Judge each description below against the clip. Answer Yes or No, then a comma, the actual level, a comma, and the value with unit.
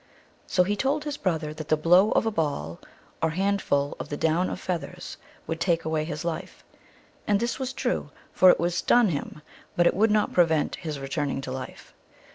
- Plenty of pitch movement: No, average, 4.6 semitones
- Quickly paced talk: Yes, fast, 210 wpm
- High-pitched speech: No, medium, 170 Hz